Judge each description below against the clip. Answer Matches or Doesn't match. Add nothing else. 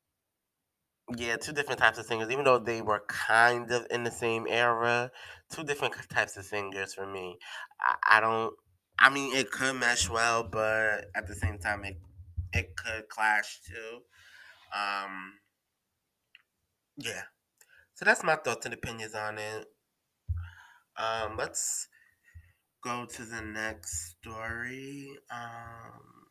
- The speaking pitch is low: Matches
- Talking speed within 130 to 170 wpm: Matches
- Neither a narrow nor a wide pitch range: Matches